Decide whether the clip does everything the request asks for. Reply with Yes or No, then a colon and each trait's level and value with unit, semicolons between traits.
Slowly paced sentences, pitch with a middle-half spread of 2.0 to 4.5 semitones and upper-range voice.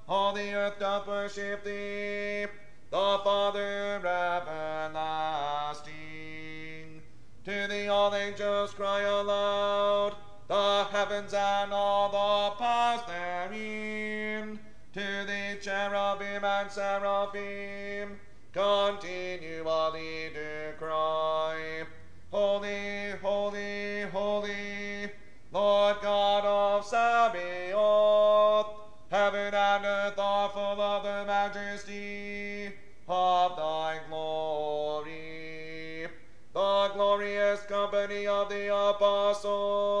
Yes: slow, 80 wpm; narrow, 2.4 semitones; high, 200 Hz